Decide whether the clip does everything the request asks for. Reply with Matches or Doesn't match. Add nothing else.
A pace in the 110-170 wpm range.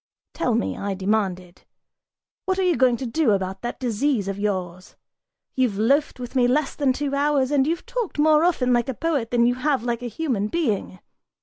Doesn't match